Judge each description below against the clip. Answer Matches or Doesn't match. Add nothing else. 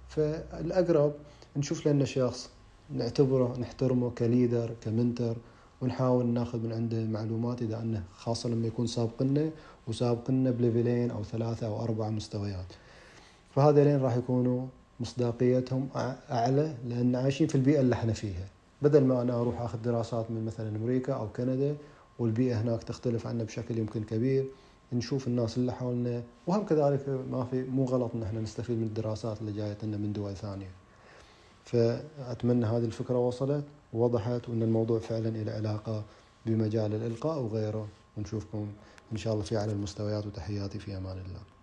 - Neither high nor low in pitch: Doesn't match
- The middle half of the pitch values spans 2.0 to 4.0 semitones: Matches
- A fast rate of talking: Matches